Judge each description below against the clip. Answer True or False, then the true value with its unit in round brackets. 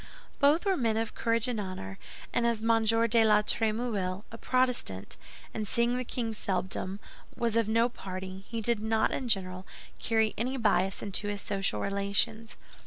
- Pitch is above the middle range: True (220 Hz)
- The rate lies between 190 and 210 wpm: False (160 wpm)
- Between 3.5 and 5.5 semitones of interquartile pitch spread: False (2.9 semitones)